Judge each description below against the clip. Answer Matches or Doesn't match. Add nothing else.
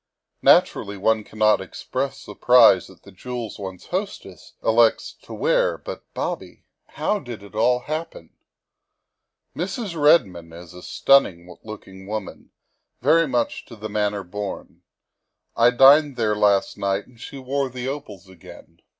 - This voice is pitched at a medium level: Doesn't match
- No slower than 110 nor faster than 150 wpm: Matches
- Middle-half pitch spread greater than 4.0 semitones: Matches